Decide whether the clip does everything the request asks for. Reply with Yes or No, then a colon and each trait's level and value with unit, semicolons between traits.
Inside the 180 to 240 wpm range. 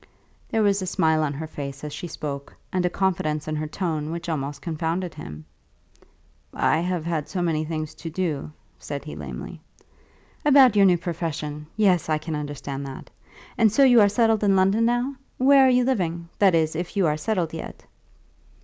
Yes: average, 190 wpm